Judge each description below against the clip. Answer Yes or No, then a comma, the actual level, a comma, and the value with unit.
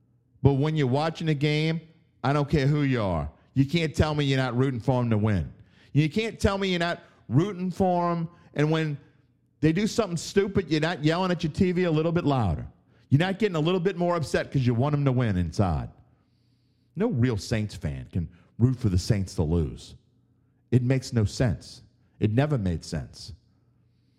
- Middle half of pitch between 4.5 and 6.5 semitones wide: Yes, wide, 5.6 semitones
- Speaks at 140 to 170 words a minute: No, fast, 205 wpm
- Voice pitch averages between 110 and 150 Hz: Yes, low, 135 Hz